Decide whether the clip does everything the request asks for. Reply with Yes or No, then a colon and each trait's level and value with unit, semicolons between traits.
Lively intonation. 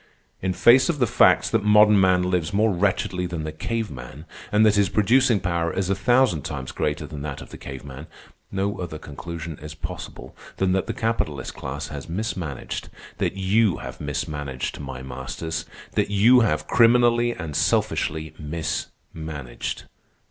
Yes: wide, 5.8 semitones